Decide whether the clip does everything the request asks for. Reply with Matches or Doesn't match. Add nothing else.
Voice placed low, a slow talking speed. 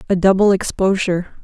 Doesn't match